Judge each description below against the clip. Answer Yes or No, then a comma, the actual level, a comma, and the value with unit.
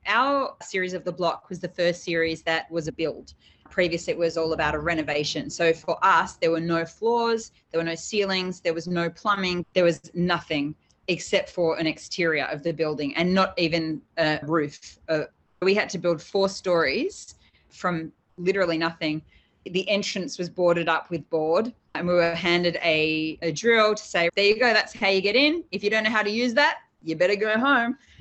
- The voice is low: No, medium, 175 Hz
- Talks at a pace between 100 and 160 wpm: No, fast, 205 wpm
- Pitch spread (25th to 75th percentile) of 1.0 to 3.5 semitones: Yes, average, 3.1 semitones